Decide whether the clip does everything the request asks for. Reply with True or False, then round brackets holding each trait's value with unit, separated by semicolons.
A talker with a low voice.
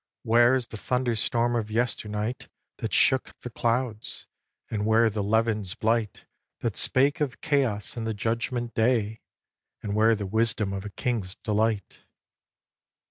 True (115 Hz)